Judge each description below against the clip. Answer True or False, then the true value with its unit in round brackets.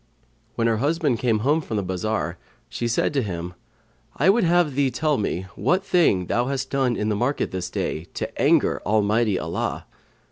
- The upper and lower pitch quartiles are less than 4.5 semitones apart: False (5.5 semitones)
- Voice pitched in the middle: False (120 Hz)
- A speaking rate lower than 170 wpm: False (185 wpm)